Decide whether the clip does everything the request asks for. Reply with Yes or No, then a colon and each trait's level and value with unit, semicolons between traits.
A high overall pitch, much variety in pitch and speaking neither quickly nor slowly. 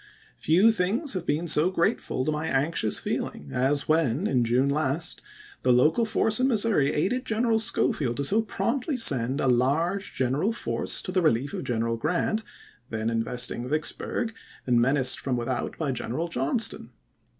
No: medium, 150 Hz; wide, 7.7 semitones; average, 165 wpm